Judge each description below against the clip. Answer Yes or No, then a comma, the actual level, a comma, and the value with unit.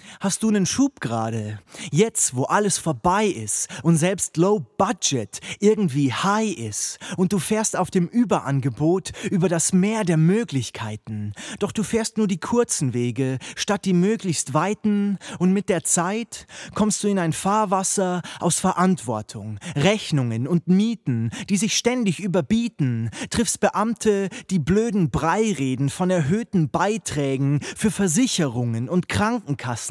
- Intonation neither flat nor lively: No, wide, 6.4 semitones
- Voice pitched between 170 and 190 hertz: Yes, medium, 185 Hz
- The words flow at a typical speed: Yes, average, 140 wpm